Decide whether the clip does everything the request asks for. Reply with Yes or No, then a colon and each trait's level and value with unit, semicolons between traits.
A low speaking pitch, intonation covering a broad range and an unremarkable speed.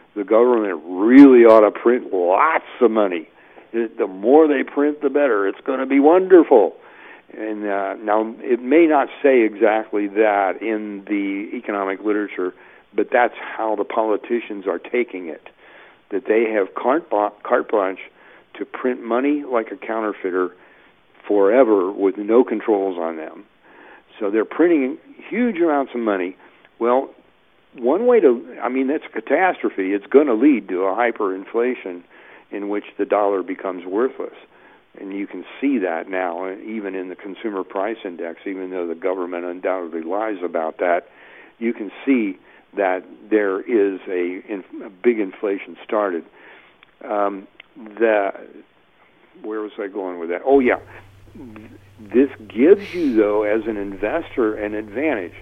Yes: low, 110 Hz; wide, 6.3 semitones; average, 150 wpm